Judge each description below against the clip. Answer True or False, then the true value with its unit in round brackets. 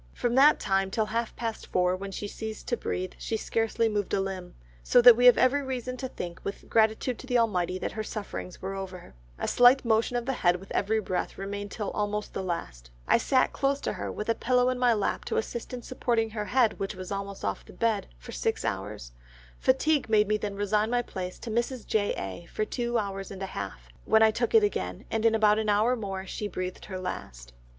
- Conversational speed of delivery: False (230 wpm)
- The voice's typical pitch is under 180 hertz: False (215 Hz)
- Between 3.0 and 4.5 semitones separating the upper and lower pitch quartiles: True (3.7 semitones)